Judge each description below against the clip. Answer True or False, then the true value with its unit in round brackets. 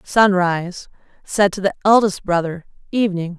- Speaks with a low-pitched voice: False (190 Hz)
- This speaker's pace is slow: True (125 wpm)